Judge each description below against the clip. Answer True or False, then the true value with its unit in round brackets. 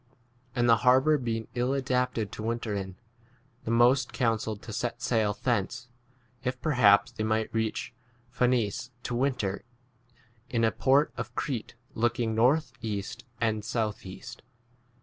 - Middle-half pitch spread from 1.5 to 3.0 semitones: True (2.5 semitones)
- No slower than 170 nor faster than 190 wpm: False (145 wpm)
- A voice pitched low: True (115 Hz)